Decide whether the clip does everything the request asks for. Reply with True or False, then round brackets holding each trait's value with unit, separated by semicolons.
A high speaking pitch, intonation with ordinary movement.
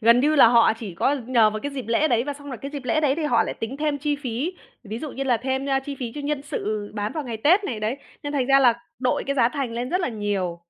True (260 Hz; 4.0 semitones)